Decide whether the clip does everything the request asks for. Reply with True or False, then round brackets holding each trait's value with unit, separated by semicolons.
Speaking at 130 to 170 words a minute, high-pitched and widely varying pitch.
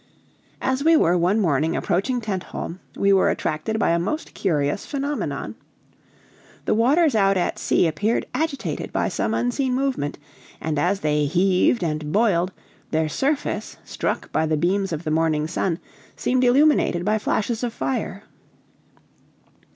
True (145 wpm; 195 Hz; 7.1 semitones)